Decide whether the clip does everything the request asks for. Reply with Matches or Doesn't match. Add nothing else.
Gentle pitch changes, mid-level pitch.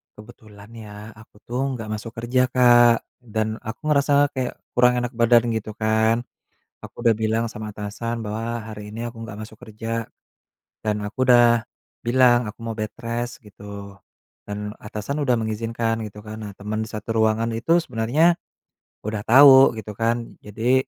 Doesn't match